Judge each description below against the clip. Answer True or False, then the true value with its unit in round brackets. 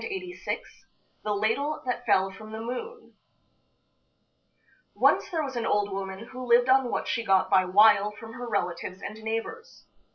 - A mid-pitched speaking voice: False (225 Hz)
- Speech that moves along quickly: False (155 wpm)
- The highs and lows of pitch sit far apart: False (4.2 semitones)